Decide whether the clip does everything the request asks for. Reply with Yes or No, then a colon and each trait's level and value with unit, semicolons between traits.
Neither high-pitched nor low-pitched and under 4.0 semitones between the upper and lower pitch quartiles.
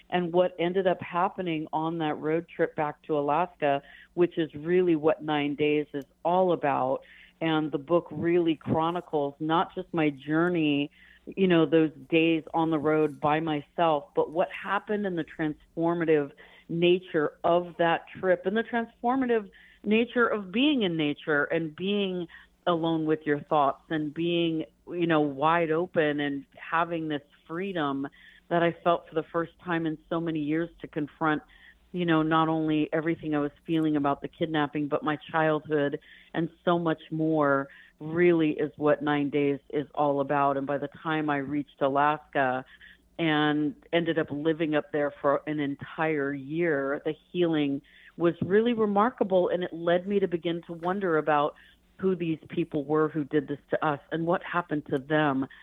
Yes: medium, 160 Hz; narrow, 2.4 semitones